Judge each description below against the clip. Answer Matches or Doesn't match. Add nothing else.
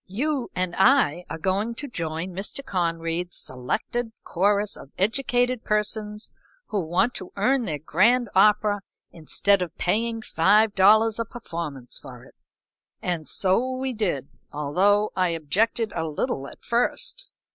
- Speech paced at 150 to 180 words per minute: Doesn't match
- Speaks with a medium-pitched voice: Doesn't match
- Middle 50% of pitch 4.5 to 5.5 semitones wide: Matches